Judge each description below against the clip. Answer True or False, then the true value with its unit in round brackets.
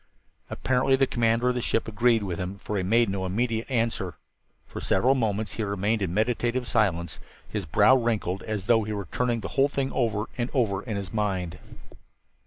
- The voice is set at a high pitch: False (110 Hz)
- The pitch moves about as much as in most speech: True (3.3 semitones)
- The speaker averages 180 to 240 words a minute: True (195 wpm)